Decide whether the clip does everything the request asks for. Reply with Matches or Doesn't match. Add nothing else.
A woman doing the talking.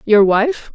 Matches